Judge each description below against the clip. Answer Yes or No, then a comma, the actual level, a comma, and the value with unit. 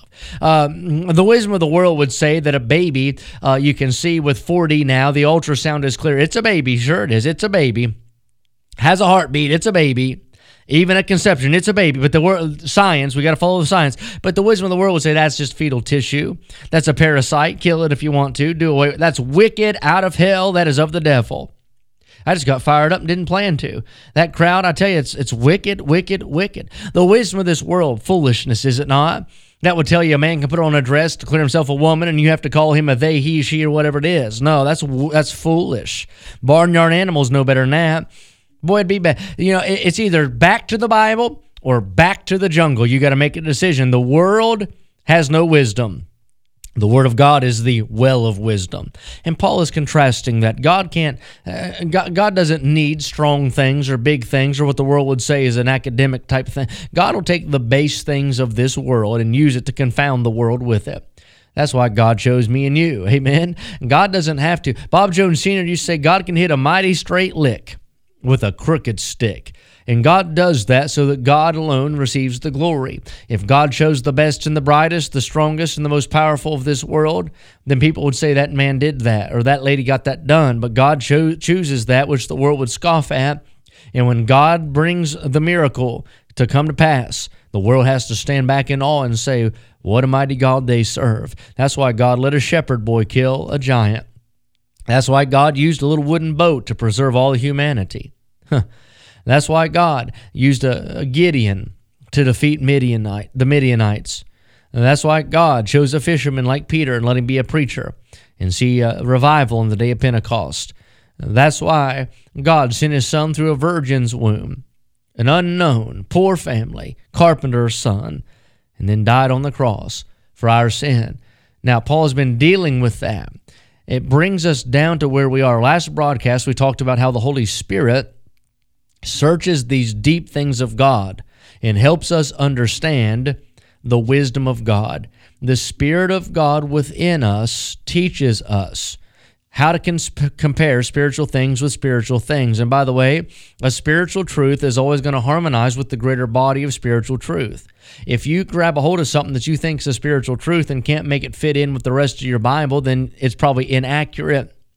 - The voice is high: No, medium, 140 Hz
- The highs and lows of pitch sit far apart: No, average, 4.0 semitones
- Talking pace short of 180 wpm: No, fast, 205 wpm